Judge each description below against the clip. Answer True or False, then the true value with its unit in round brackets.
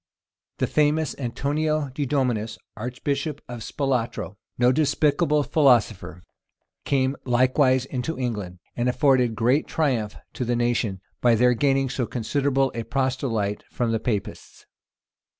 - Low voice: True (125 Hz)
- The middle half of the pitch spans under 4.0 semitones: True (3.1 semitones)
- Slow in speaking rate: True (130 wpm)